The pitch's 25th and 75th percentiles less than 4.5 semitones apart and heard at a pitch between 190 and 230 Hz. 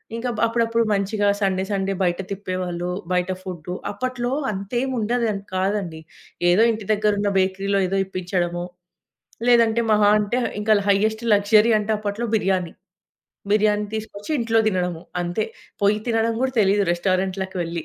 Yes: average, 2.9 semitones; high, 200 Hz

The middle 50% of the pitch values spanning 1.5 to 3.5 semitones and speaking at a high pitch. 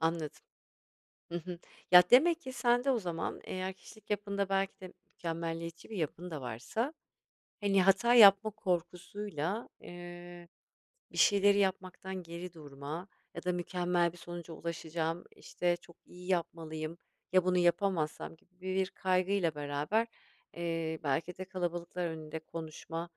No: average, 2.7 semitones; medium, 175 Hz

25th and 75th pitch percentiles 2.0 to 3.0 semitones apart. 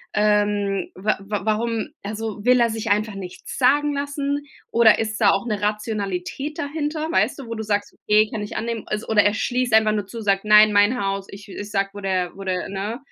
Yes: narrow, 2.5 semitones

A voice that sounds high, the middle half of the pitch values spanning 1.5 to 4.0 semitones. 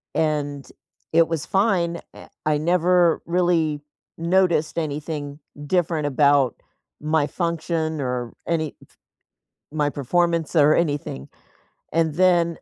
No: medium, 160 Hz; average, 2.7 semitones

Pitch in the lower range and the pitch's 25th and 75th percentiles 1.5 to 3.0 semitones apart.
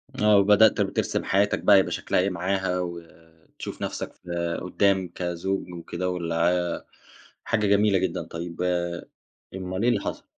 Yes: very low, 90 Hz; narrow, 2.5 semitones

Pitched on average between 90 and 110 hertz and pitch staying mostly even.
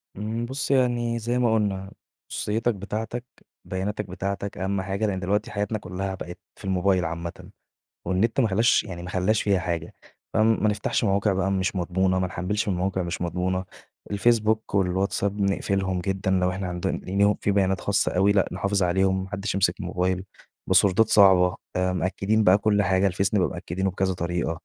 Yes: very low, 95 Hz; narrow, 2.1 semitones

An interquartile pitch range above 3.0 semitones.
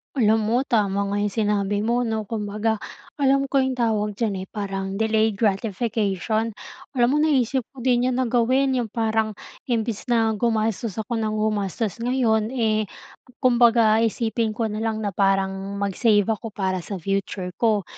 No: narrow, 2.5 semitones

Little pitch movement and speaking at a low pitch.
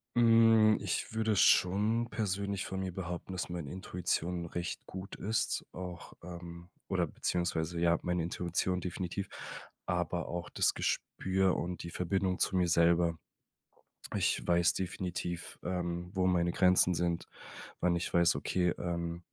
Yes: narrow, 1.5 semitones; very low, 90 Hz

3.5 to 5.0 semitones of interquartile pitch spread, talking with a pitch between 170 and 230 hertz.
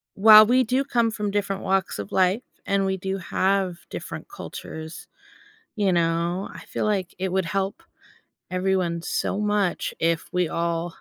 No: average, 3.0 semitones; high, 190 Hz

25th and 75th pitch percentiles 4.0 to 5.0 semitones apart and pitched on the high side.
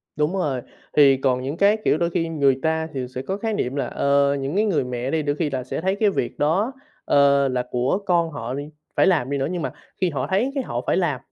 No: average, 4.6 semitones; medium, 145 Hz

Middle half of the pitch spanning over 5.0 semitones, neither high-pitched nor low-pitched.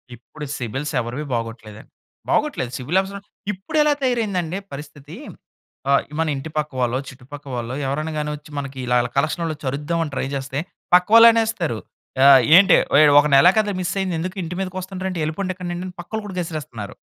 Yes: wide, 5.4 semitones; medium, 155 Hz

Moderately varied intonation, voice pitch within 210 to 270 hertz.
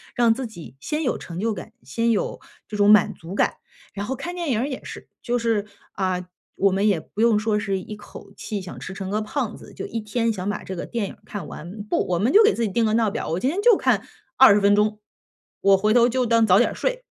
Yes: average, 3.1 semitones; high, 215 Hz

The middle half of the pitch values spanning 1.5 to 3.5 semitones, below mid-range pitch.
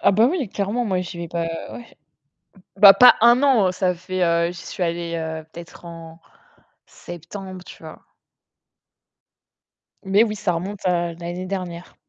No: average, 2.8 semitones; medium, 180 Hz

